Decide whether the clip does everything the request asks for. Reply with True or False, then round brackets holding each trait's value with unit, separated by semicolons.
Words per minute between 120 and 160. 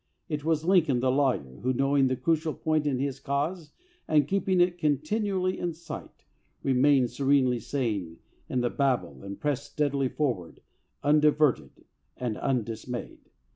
True (145 wpm)